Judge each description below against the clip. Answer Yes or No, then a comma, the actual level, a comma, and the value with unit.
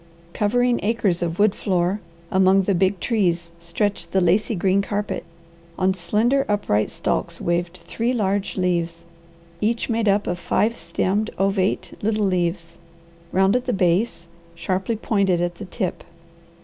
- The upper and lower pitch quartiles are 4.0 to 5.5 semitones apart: No, average, 3.2 semitones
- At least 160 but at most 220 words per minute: No, average, 145 wpm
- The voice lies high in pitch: Yes, high, 195 Hz